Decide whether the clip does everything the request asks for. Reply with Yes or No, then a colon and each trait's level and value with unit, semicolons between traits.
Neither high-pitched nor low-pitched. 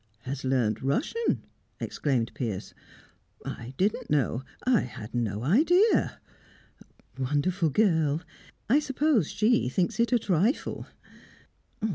Yes: medium, 160 Hz